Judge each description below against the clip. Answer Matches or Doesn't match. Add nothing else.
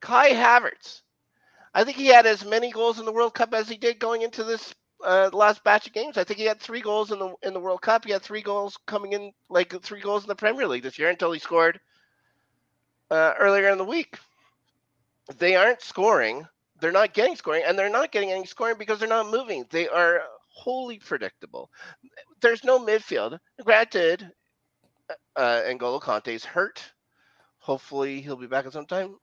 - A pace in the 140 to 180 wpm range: Doesn't match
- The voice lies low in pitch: Doesn't match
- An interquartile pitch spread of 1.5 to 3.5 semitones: Doesn't match